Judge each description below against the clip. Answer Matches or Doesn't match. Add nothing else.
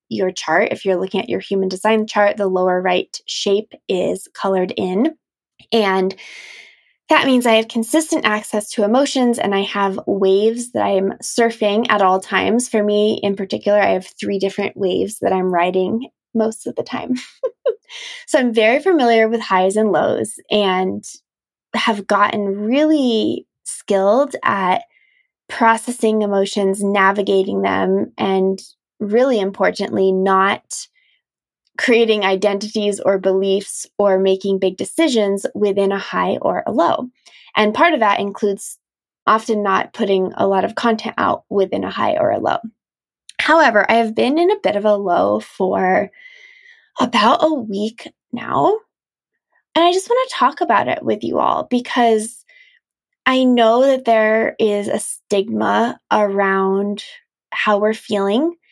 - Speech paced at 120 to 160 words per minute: Matches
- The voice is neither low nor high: Doesn't match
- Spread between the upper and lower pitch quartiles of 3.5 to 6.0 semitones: Matches